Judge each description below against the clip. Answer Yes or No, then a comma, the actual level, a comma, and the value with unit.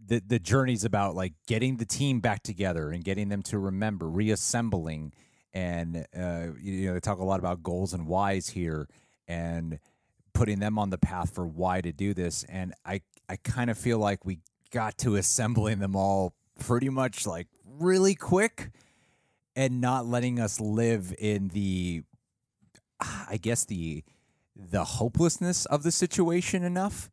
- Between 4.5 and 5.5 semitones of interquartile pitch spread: Yes, average, 4.8 semitones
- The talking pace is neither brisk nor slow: Yes, average, 165 wpm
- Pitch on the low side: Yes, low, 105 Hz